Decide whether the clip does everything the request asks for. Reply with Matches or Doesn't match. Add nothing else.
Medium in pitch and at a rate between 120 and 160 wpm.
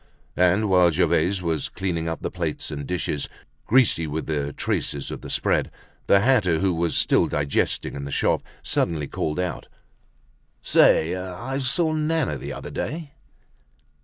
Doesn't match